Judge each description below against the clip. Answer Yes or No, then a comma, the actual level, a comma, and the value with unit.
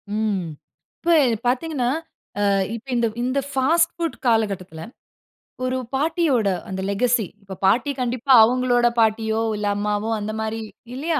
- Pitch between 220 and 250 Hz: Yes, high, 240 Hz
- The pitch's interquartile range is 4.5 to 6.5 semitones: No, average, 3.8 semitones